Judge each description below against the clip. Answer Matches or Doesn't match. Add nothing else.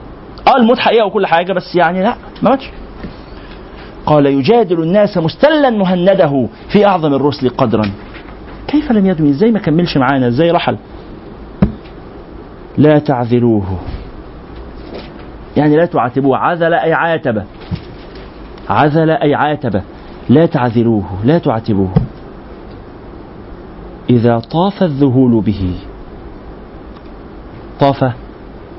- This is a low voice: Doesn't match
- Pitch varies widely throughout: Matches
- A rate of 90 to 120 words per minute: Matches